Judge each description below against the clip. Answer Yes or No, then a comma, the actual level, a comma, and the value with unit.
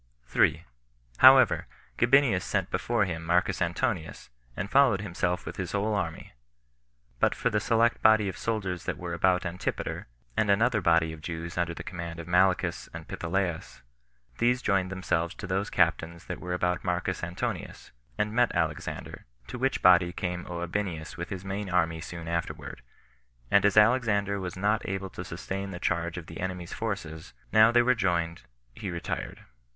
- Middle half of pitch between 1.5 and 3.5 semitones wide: Yes, average, 3.2 semitones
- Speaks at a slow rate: No, average, 165 wpm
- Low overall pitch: Yes, very low, 90 Hz